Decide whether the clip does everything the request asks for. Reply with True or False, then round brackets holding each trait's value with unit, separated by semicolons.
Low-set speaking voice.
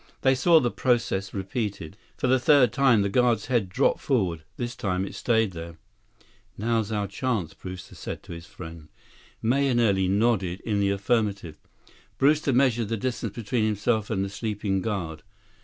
True (110 Hz)